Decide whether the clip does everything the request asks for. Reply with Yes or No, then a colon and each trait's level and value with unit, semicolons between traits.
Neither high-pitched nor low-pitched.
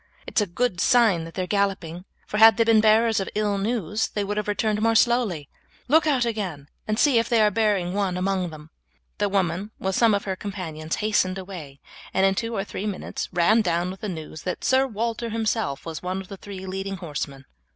No: high, 200 Hz